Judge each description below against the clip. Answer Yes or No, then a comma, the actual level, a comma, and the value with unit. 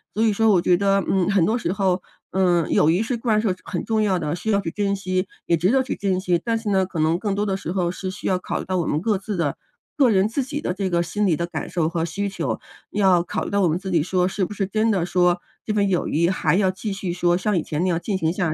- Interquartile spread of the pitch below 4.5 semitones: Yes, average, 2.8 semitones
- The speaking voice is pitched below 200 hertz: Yes, high, 190 Hz